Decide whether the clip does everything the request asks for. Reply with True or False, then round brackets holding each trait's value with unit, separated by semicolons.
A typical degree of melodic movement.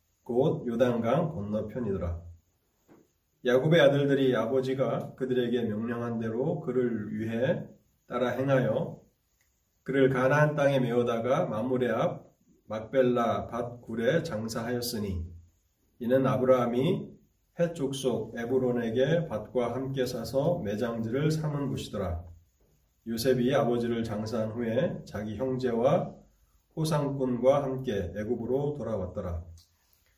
True (3.4 semitones)